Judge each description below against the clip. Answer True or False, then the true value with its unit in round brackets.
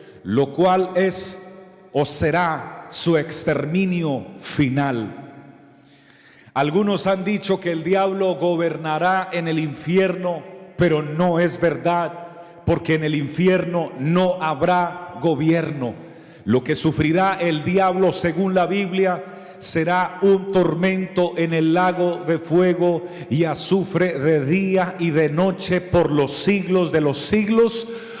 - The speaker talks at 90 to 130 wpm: True (125 wpm)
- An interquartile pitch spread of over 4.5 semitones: False (2.7 semitones)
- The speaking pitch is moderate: True (175 Hz)